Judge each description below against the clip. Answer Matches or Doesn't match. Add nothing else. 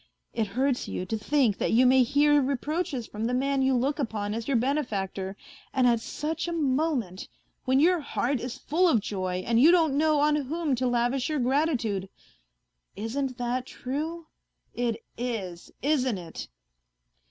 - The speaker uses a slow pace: Doesn't match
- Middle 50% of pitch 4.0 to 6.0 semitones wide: Matches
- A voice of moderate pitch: Doesn't match